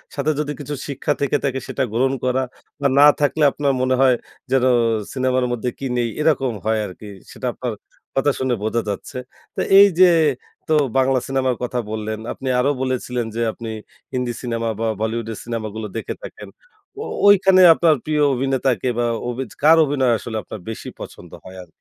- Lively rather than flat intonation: No, average, 3.0 semitones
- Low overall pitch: Yes, low, 130 Hz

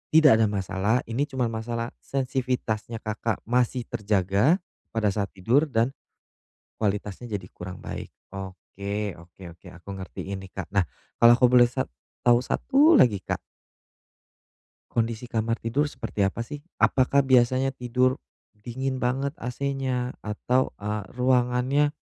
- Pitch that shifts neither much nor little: Yes, average, 3.9 semitones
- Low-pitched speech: Yes, low, 120 Hz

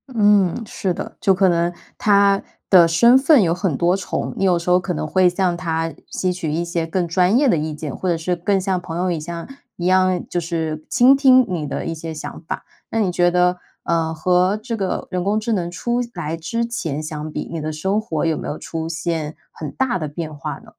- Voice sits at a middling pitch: Yes, medium, 175 Hz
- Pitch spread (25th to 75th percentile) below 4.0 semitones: Yes, average, 3.0 semitones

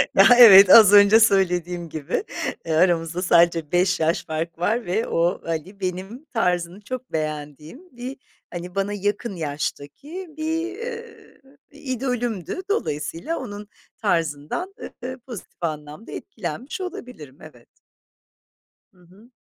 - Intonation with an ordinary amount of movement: No, wide, 6.9 semitones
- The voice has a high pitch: Yes, high, 195 Hz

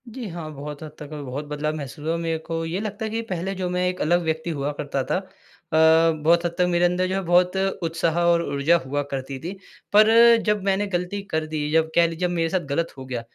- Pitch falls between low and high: Yes, medium, 165 Hz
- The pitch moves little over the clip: No, average, 3.0 semitones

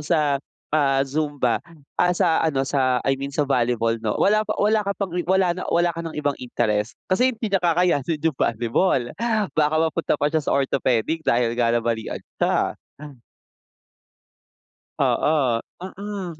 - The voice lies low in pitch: No, medium, 150 Hz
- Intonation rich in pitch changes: Yes, wide, 5.7 semitones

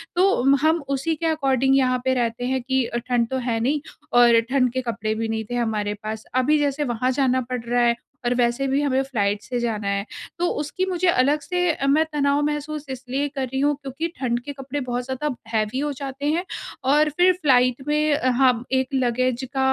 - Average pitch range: Yes, average, 3.2 semitones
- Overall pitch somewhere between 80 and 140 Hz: No, very high, 265 Hz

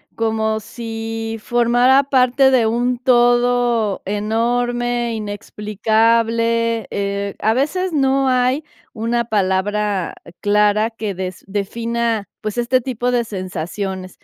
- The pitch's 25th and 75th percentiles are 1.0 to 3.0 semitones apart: Yes, narrow, 2.6 semitones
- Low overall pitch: No, high, 230 Hz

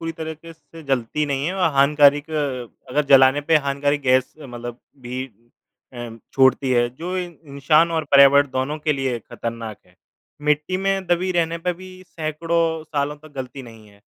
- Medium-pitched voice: Yes, medium, 145 Hz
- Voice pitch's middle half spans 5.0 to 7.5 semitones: No, average, 3.8 semitones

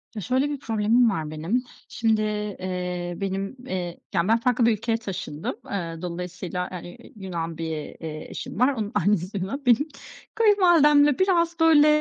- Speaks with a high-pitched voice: Yes, high, 210 Hz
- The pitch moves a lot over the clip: Yes, wide, 6.0 semitones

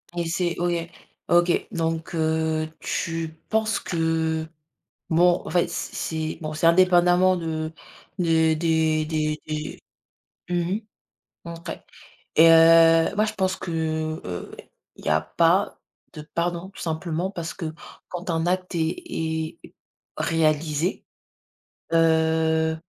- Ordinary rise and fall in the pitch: No, narrow, 1.6 semitones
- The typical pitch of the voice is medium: Yes, medium, 165 Hz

